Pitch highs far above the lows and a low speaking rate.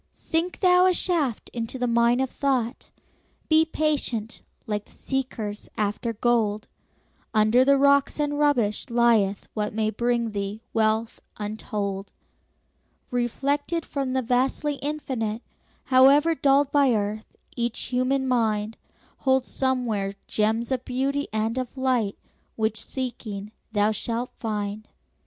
No: average, 3.9 semitones; slow, 125 wpm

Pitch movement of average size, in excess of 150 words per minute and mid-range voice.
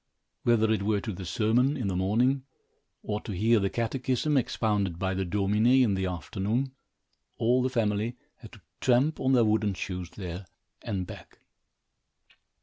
No: average, 4.2 semitones; average, 160 wpm; low, 110 Hz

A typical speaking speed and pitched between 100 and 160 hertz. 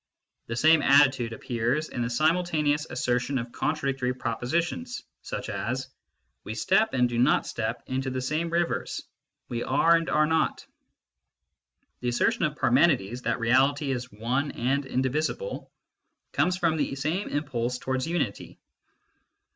Yes: average, 145 wpm; low, 135 Hz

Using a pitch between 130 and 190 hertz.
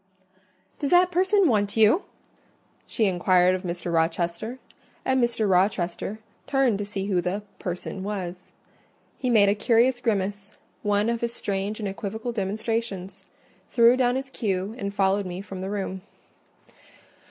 No: high, 205 Hz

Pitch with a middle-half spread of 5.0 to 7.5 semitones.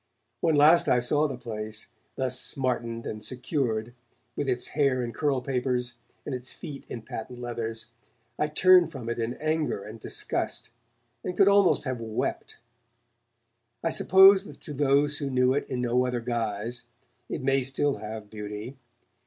No: average, 3.8 semitones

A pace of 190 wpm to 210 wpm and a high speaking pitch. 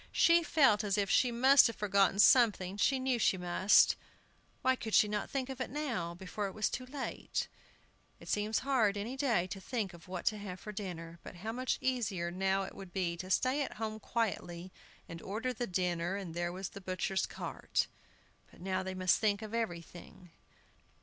Yes: average, 195 wpm; high, 205 Hz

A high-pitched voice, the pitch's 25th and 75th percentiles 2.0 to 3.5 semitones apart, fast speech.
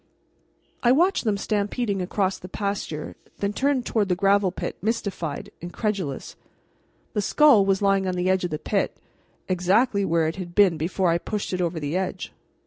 No: high, 195 Hz; average, 2.7 semitones; average, 175 wpm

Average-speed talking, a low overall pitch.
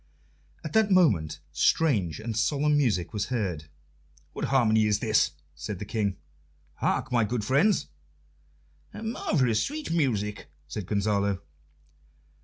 No: slow, 120 wpm; low, 110 Hz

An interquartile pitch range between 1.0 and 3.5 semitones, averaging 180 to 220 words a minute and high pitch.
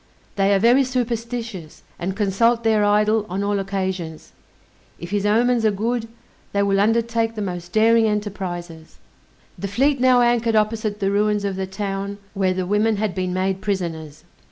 No: average, 2.9 semitones; average, 165 wpm; high, 205 Hz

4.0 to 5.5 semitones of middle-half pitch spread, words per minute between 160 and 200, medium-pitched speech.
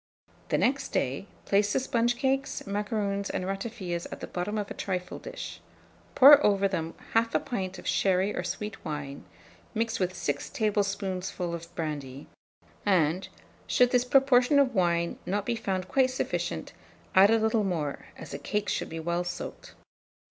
No: average, 4.4 semitones; average, 165 wpm; high, 200 Hz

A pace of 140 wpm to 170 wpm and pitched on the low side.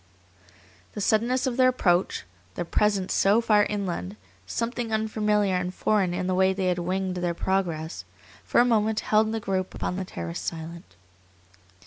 No: average, 160 wpm; high, 195 Hz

